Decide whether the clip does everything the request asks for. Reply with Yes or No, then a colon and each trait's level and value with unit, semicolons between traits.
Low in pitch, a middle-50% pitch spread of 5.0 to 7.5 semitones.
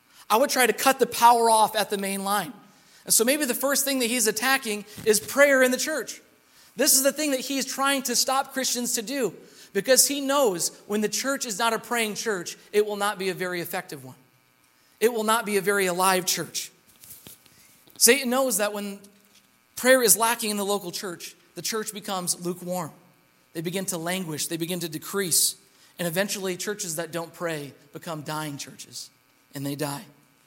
No: high, 205 Hz; wide, 5.4 semitones